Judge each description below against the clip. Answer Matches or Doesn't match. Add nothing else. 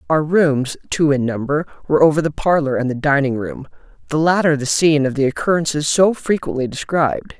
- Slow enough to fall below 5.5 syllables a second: Doesn't match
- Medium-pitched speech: Matches